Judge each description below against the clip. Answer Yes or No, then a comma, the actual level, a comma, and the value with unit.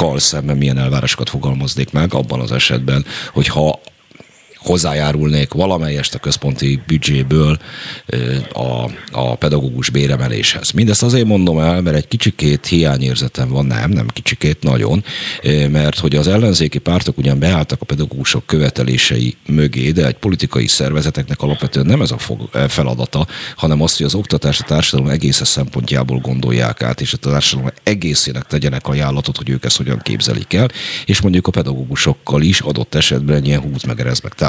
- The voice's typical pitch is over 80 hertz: No, very low, 70 Hz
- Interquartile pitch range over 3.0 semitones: No, average, 2.7 semitones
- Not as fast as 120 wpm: No, average, 145 wpm